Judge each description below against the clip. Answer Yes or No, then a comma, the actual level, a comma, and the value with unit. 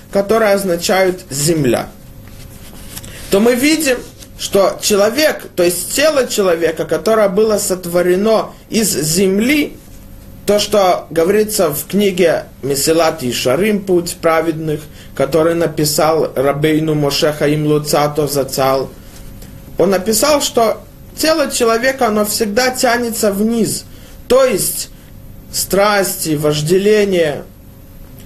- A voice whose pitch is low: No, medium, 180 Hz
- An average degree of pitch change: No, wide, 6.2 semitones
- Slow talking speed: Yes, slow, 100 wpm